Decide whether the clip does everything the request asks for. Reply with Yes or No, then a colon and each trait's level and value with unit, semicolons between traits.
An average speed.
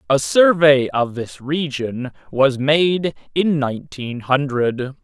No: slow, 120 wpm